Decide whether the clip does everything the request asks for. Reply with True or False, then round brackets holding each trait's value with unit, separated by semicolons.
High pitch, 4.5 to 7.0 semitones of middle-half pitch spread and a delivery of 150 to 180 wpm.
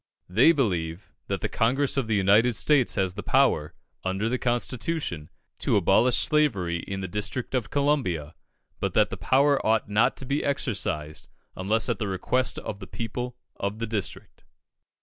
False (110 Hz; 5.2 semitones; 170 wpm)